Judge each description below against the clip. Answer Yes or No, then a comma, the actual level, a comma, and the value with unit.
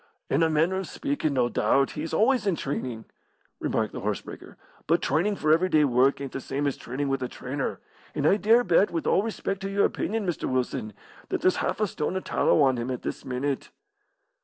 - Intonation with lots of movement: Yes, wide, 6.6 semitones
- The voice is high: No, medium, 150 Hz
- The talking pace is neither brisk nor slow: No, fast, 220 wpm